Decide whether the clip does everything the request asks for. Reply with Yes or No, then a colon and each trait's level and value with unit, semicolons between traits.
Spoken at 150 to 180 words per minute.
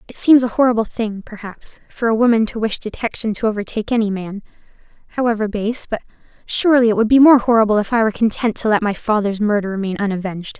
No: fast, 205 wpm